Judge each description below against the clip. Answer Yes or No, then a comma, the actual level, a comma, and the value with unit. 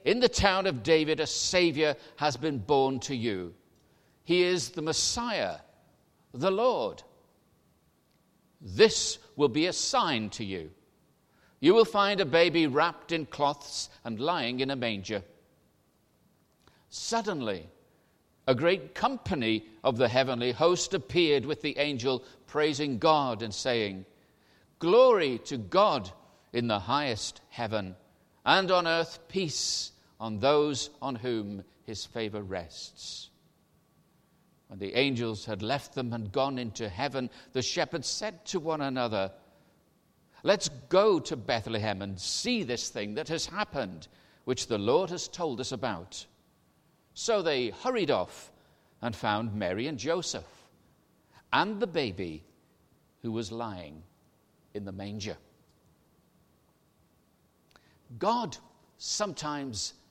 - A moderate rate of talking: No, slow, 125 wpm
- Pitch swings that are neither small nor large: No, wide, 7.0 semitones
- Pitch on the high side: No, low, 135 Hz